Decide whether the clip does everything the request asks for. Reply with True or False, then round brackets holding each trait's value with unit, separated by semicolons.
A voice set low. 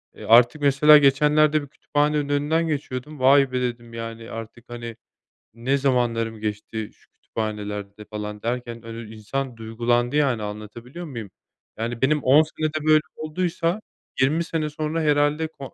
True (130 Hz)